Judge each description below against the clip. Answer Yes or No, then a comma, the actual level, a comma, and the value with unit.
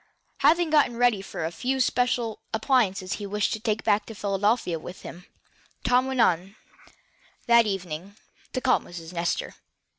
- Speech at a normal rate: Yes, average, 150 wpm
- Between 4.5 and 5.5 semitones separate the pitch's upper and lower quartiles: Yes, average, 4.8 semitones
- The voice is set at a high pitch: Yes, high, 210 Hz